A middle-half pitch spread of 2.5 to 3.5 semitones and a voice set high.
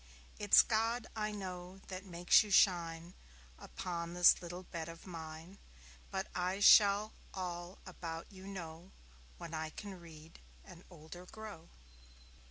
No: average, 2.8 semitones; medium, 180 Hz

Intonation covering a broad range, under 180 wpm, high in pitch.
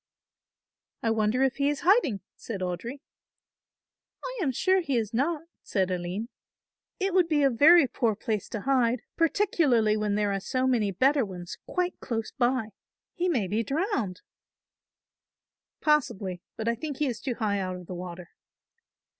Yes: wide, 6.3 semitones; average, 165 wpm; high, 235 Hz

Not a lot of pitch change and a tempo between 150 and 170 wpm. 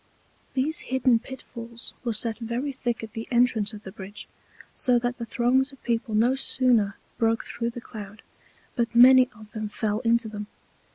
No: narrow, 2.3 semitones; average, 180 wpm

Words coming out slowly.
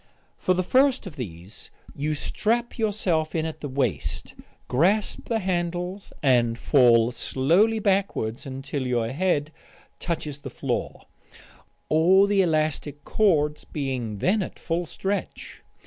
Yes: slow, 130 wpm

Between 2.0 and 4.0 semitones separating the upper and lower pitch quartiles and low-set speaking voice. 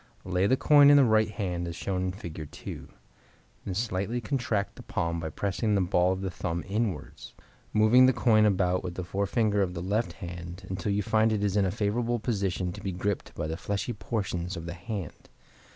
Yes: average, 3.4 semitones; low, 100 Hz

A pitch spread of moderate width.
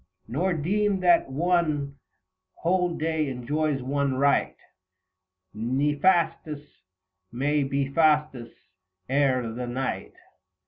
Yes: average, 3.6 semitones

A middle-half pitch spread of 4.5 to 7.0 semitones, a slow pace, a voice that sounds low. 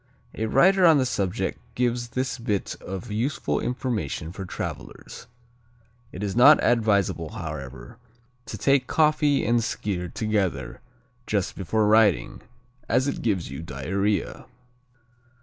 Yes: average, 4.9 semitones; slow, 125 wpm; low, 110 Hz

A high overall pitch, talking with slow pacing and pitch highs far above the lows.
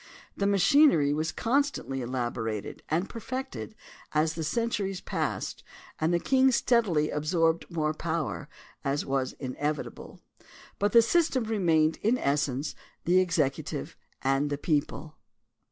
No: medium, 160 Hz; slow, 120 wpm; wide, 6.5 semitones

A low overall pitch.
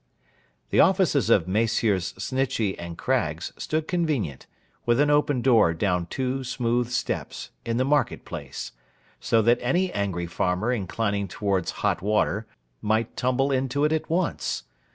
Yes: low, 120 Hz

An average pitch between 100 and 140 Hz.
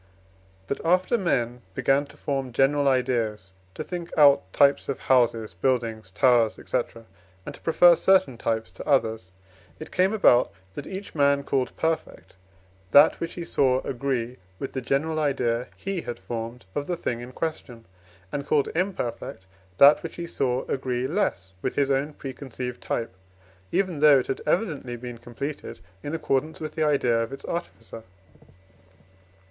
Yes: low, 135 Hz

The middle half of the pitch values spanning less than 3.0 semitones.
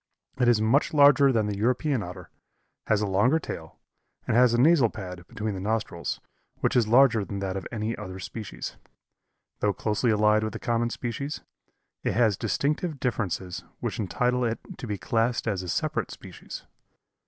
No: average, 3.6 semitones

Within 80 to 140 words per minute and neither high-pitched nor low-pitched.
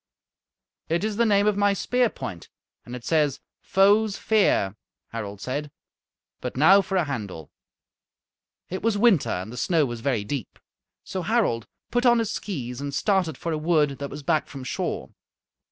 No: average, 170 wpm; medium, 155 Hz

